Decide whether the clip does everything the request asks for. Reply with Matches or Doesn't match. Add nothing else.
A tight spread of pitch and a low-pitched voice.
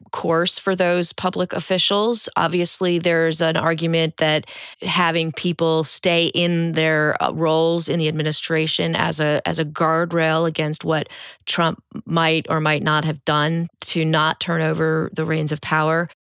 Doesn't match